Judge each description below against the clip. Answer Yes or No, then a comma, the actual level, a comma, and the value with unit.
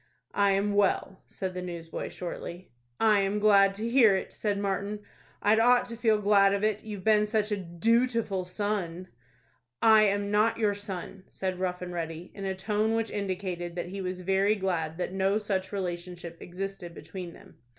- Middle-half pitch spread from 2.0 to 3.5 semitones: Yes, narrow, 2.5 semitones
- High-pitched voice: Yes, high, 195 Hz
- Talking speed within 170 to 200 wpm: Yes, average, 180 wpm